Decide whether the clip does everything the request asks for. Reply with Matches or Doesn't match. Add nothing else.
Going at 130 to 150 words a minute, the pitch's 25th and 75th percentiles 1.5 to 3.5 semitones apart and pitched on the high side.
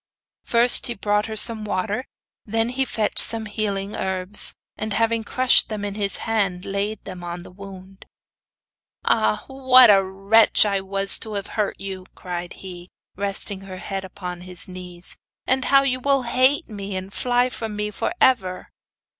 Doesn't match